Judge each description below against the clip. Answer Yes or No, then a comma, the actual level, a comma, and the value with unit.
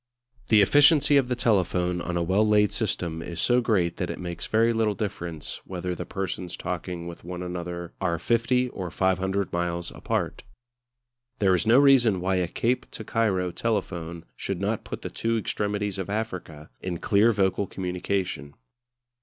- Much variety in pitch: No, average, 3.9 semitones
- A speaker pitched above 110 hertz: No, very low, 95 Hz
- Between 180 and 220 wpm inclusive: No, average, 170 wpm